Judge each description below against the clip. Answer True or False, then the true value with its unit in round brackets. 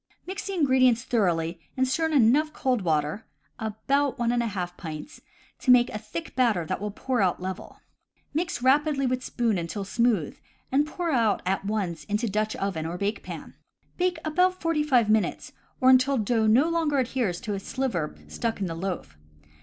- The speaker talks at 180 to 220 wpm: True (185 wpm)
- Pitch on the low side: False (235 Hz)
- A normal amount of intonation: False (5.7 semitones)